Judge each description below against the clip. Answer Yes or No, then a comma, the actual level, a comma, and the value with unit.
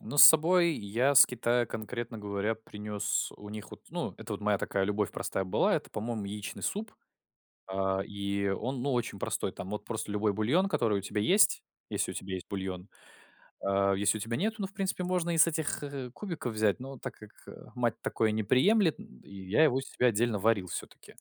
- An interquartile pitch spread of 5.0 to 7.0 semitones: Yes, wide, 5.5 semitones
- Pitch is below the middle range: Yes, low, 110 Hz